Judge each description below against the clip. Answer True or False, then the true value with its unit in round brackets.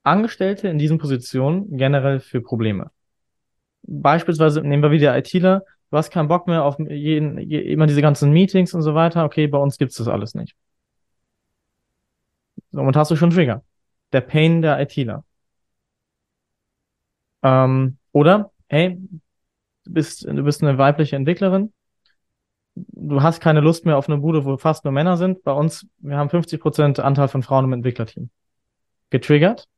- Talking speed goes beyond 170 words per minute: False (155 wpm)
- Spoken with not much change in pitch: False (3.3 semitones)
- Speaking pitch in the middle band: True (150 Hz)